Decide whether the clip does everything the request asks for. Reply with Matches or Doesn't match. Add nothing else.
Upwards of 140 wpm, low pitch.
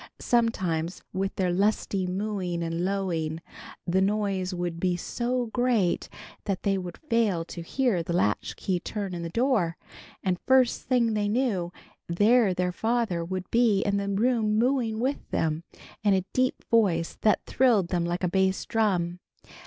Doesn't match